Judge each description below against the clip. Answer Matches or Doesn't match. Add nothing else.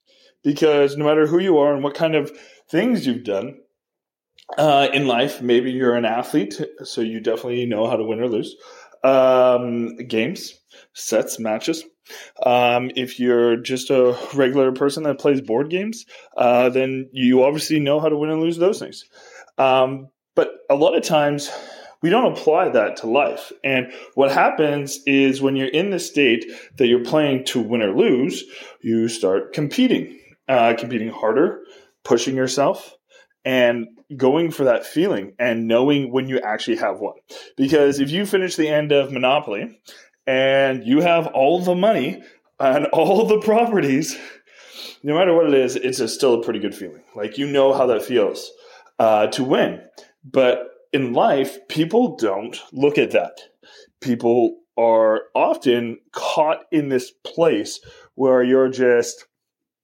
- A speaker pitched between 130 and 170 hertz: Matches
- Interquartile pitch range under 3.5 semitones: Doesn't match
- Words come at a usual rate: Matches